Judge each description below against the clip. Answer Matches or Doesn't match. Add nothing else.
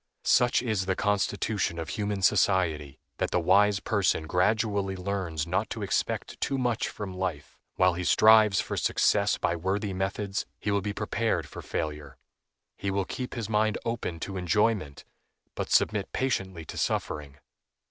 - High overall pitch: Doesn't match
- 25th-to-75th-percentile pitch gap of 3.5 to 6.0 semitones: Doesn't match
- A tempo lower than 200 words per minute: Matches